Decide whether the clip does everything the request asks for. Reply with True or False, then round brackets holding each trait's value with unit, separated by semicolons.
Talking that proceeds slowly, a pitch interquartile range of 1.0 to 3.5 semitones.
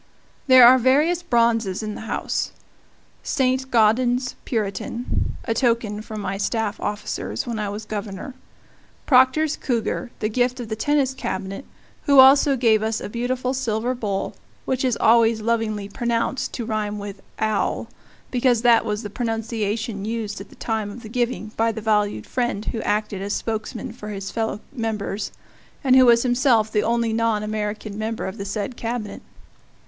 False (165 wpm; 2.7 semitones)